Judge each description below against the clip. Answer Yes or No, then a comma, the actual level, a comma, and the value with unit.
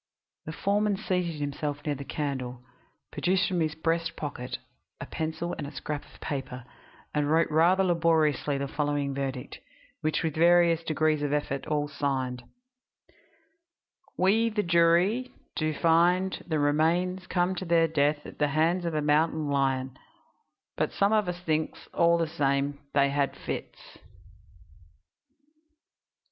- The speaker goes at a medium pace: Yes, average, 145 wpm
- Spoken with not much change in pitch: No, average, 3.1 semitones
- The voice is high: No, medium, 155 Hz